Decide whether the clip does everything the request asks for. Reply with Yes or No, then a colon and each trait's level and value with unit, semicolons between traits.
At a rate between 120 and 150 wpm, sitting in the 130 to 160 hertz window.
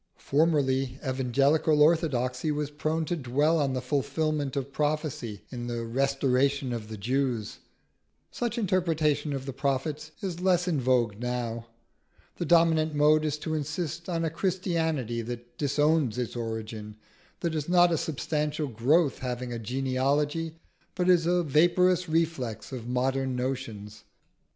Yes: average, 140 wpm; medium, 140 Hz